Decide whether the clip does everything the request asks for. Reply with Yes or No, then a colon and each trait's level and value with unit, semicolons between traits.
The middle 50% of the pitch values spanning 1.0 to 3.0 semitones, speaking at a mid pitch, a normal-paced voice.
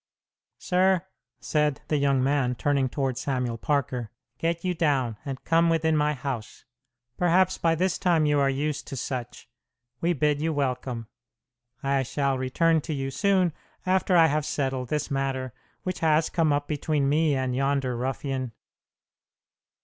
No: average, 3.5 semitones; medium, 145 Hz; average, 155 wpm